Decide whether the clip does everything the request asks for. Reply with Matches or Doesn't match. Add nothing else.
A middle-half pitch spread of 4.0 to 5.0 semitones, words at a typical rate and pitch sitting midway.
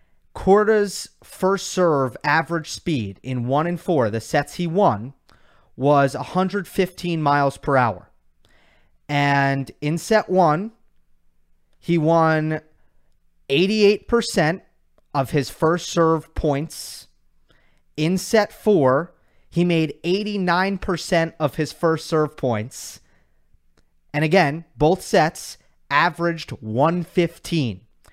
Doesn't match